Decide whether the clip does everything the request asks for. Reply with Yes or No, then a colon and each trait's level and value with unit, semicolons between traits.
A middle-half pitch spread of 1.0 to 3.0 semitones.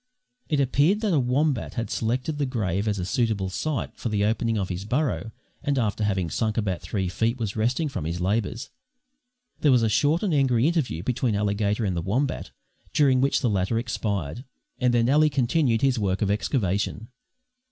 No: average, 4.9 semitones